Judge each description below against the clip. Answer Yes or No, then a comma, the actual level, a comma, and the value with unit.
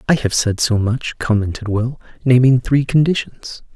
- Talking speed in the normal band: Yes, average, 160 wpm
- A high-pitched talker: No, low, 120 Hz